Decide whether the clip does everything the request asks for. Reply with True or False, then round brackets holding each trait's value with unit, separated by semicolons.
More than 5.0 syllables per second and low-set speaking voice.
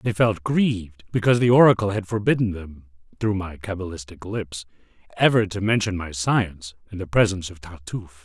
True (5.7 syllables/s; 95 Hz)